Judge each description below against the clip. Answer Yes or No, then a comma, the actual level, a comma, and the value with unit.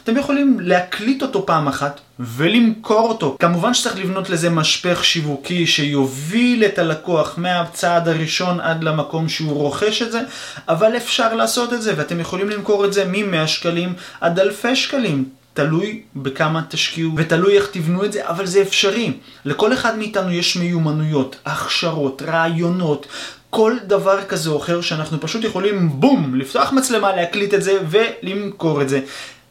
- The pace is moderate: No, fast, 155 wpm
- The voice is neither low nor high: Yes, medium, 175 Hz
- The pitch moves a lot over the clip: No, average, 4.8 semitones